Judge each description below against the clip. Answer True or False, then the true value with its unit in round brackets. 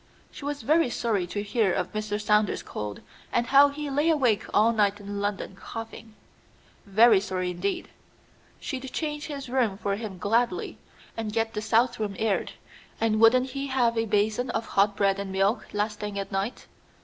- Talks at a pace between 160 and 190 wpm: True (180 wpm)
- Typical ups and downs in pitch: True (3.5 semitones)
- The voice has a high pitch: True (220 Hz)